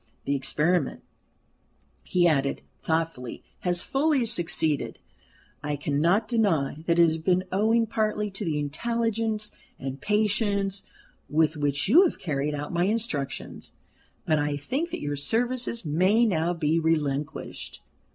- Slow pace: Yes, slow, 130 wpm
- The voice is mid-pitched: Yes, medium, 170 Hz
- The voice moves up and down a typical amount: No, wide, 6.5 semitones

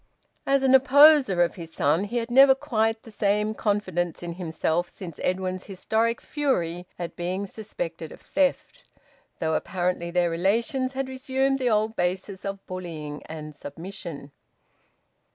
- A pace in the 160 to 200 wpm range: No, average, 150 wpm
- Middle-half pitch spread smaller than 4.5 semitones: No, wide, 5.6 semitones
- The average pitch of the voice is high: Yes, high, 195 Hz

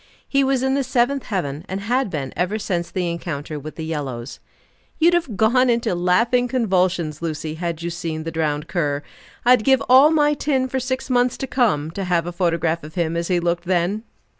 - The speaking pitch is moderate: Yes, medium, 180 Hz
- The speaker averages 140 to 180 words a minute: No, fast, 205 wpm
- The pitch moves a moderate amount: No, wide, 7.3 semitones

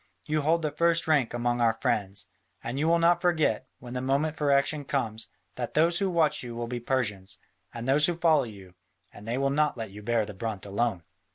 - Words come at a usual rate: No, fast, 220 wpm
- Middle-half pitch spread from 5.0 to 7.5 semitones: Yes, average, 5.3 semitones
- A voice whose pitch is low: Yes, low, 130 Hz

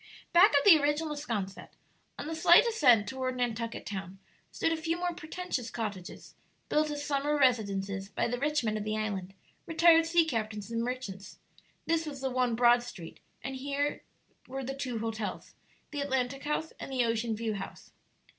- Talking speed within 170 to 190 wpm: Yes, average, 175 wpm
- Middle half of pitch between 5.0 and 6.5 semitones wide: Yes, average, 5.3 semitones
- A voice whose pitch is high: Yes, very high, 255 Hz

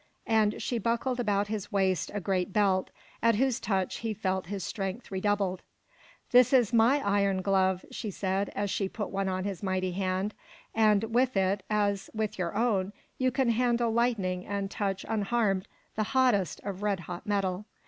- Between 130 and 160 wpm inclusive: No, average, 175 wpm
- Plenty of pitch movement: No, average, 2.8 semitones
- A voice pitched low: No, high, 205 Hz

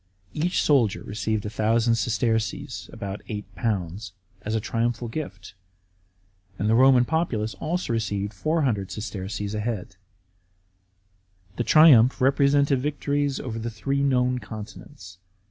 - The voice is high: No, low, 115 Hz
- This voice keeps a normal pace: No, slow, 115 wpm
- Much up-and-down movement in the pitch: No, average, 4.5 semitones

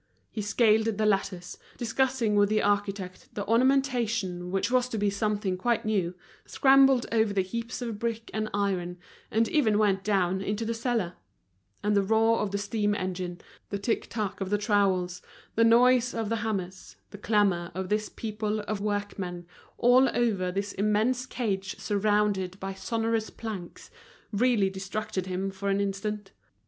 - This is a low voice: No, high, 210 Hz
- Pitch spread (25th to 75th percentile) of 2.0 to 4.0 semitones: Yes, average, 2.8 semitones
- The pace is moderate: Yes, average, 160 wpm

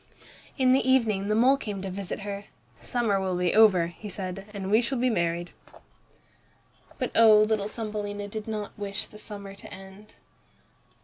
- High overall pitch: Yes, high, 205 Hz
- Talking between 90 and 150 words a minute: No, average, 175 wpm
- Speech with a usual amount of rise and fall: No, narrow, 2.2 semitones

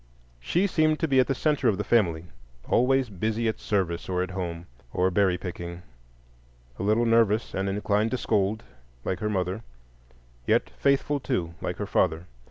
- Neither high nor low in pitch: No, low, 105 Hz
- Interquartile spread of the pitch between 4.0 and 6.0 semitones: Yes, average, 4.6 semitones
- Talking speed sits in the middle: Yes, average, 170 wpm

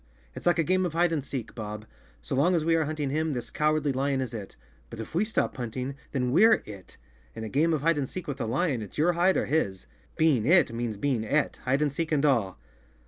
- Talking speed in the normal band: No, fast, 250 wpm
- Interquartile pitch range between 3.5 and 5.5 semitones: Yes, average, 5.2 semitones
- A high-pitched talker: No, medium, 140 Hz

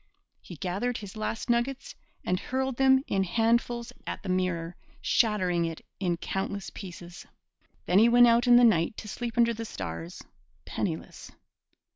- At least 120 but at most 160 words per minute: Yes, average, 155 wpm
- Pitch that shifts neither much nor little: Yes, average, 4.8 semitones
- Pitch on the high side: Yes, high, 215 Hz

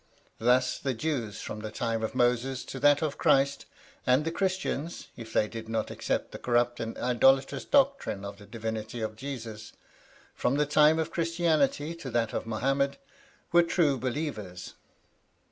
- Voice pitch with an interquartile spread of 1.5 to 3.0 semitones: No, average, 4.8 semitones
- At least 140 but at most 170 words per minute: Yes, average, 160 wpm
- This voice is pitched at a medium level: No, low, 130 Hz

